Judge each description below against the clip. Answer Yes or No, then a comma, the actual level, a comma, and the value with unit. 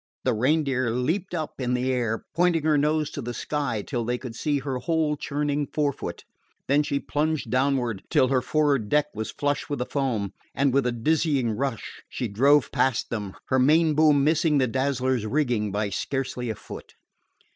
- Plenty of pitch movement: No, average, 3.4 semitones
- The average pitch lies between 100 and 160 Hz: Yes, low, 135 Hz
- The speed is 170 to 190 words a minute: Yes, average, 185 wpm